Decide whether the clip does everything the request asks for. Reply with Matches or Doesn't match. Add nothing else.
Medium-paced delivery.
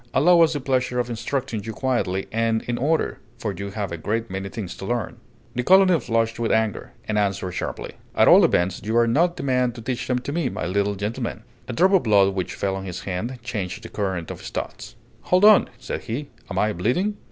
Doesn't match